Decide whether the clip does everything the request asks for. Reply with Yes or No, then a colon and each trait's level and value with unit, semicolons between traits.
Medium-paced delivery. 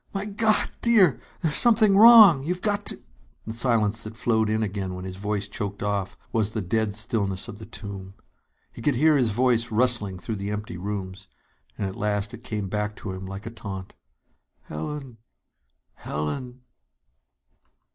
Yes: average, 170 wpm